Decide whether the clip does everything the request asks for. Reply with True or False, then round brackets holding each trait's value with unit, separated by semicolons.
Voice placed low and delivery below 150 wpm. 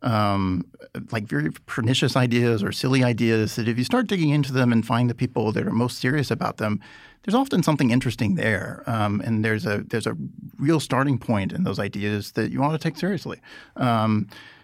False (120 Hz; 200 wpm)